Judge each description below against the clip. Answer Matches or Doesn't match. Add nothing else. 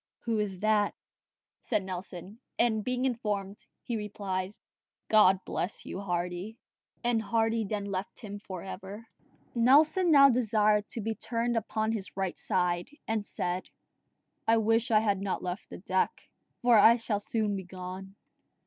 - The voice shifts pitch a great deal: Doesn't match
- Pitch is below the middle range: Doesn't match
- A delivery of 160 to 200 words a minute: Doesn't match